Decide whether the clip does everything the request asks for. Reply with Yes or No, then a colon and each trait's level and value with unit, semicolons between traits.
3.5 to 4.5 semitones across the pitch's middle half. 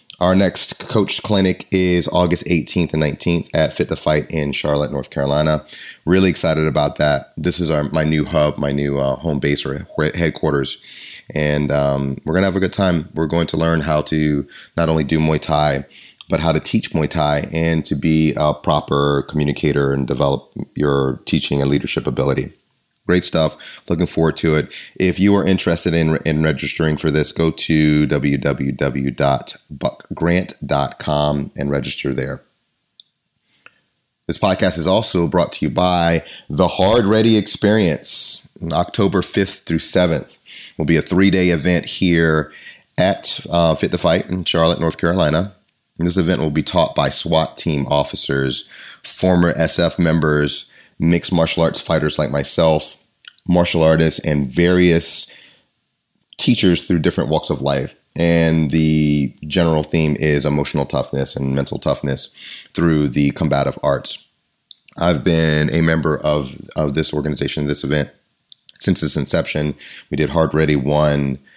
No: narrow, 2.6 semitones